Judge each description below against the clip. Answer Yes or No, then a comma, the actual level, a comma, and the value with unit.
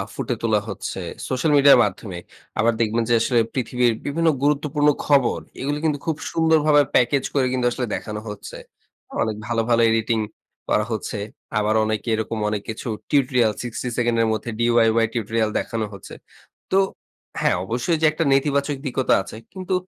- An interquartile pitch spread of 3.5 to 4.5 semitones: Yes, average, 4.2 semitones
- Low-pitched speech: Yes, low, 120 Hz